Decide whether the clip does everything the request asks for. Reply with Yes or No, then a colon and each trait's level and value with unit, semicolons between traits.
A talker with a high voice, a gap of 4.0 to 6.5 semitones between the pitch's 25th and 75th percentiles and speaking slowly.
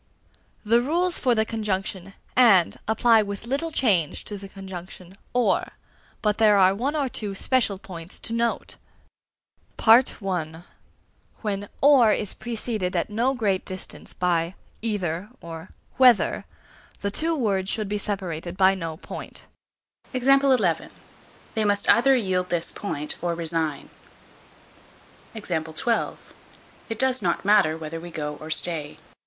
Yes: high, 200 Hz; average, 5.0 semitones; slow, 130 wpm